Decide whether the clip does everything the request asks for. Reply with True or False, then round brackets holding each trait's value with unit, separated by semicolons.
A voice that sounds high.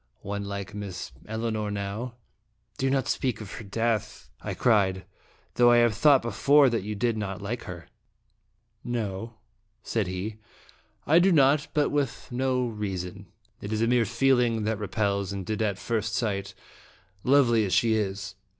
False (110 Hz)